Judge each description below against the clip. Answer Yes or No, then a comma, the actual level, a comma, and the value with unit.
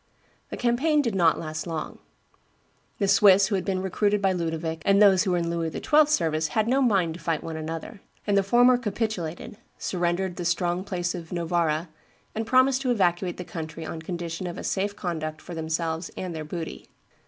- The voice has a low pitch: No, medium, 180 Hz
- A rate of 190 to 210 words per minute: Yes, average, 195 wpm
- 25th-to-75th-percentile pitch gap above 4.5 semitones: No, average, 3.6 semitones